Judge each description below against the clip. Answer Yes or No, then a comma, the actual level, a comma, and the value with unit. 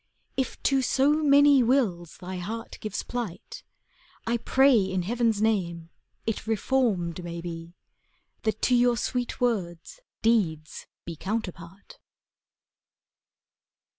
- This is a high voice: Yes, high, 220 Hz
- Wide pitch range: Yes, wide, 6.0 semitones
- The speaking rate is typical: No, slow, 110 wpm